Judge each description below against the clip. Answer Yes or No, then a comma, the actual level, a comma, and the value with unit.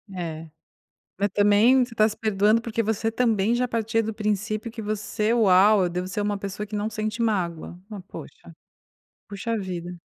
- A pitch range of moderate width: No, narrow, 2.2 semitones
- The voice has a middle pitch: No, high, 210 Hz